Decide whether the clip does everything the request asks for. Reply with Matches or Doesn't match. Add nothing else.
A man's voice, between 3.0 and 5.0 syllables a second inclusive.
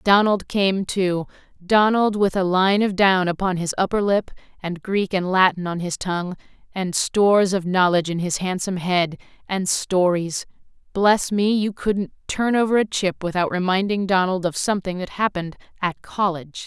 Doesn't match